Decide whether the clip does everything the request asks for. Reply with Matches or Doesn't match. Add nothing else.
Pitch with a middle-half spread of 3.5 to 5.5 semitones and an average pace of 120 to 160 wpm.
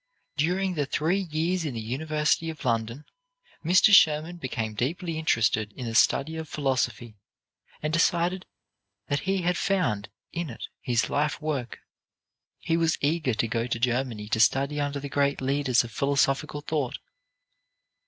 Matches